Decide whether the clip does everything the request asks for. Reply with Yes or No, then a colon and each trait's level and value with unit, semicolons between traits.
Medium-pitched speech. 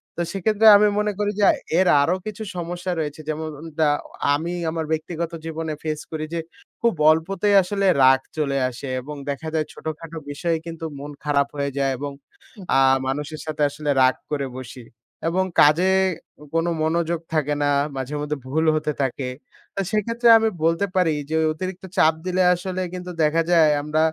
Yes: medium, 160 Hz